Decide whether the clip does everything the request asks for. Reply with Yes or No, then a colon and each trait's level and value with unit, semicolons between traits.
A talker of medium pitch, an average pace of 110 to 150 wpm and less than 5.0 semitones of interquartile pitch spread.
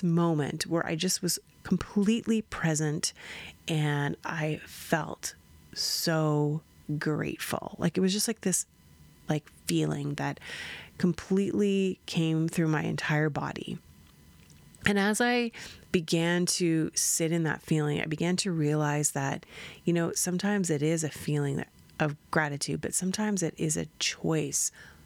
Yes: medium, 160 Hz; slow, 135 wpm; average, 3.4 semitones